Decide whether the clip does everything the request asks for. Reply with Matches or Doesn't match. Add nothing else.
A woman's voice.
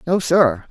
Doesn't match